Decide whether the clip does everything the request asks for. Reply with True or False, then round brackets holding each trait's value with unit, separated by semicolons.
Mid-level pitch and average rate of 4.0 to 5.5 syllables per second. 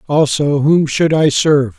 True (145 Hz; 4.4 syllables/s)